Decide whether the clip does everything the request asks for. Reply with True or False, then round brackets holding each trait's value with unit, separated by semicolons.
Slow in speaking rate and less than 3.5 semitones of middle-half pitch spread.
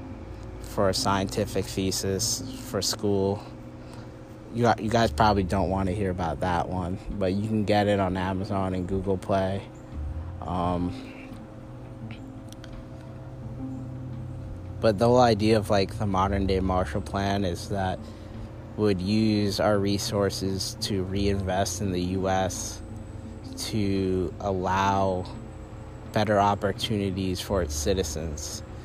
True (125 wpm; 2.5 semitones)